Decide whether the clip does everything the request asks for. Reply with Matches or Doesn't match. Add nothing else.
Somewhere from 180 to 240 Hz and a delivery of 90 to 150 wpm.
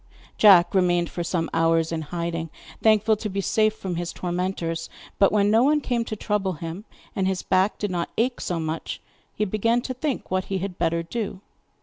Doesn't match